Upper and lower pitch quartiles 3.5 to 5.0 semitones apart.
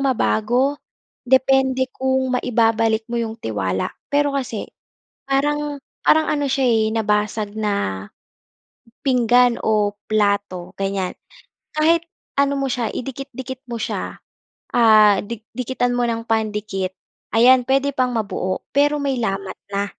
Yes: average, 4.0 semitones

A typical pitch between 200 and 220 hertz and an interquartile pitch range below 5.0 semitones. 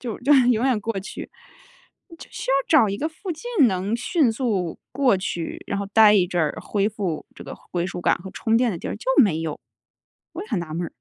No: high, 215 Hz; wide, 5.6 semitones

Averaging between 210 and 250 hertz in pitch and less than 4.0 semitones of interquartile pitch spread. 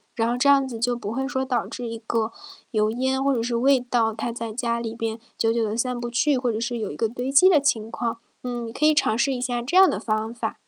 Yes: high, 240 Hz; narrow, 2.5 semitones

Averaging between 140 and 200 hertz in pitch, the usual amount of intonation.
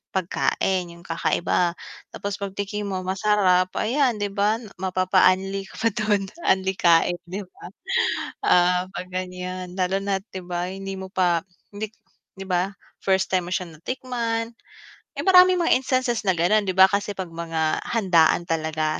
No: high, 190 Hz; narrow, 2.3 semitones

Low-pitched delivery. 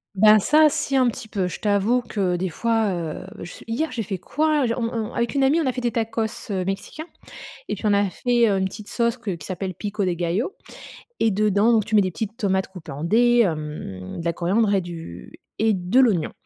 No: high, 210 Hz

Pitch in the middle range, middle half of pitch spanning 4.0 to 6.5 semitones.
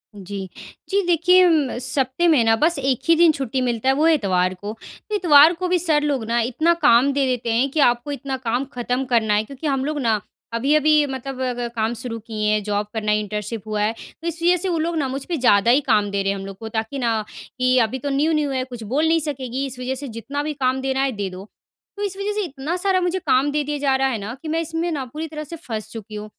No: very high, 265 Hz; average, 5.2 semitones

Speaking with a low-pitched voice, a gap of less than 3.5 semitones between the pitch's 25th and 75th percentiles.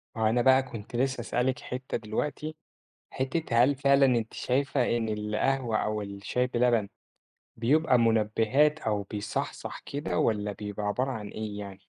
No: low, 120 Hz; average, 3.8 semitones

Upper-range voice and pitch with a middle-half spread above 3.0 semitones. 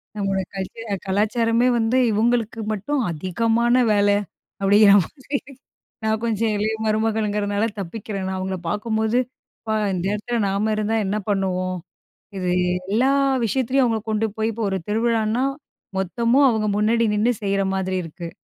No: high, 215 Hz; narrow, 2.6 semitones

